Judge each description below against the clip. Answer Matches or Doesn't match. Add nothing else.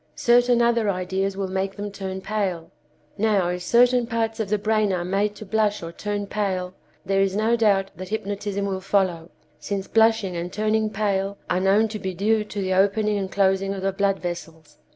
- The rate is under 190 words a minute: Doesn't match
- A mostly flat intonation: Matches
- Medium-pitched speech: Doesn't match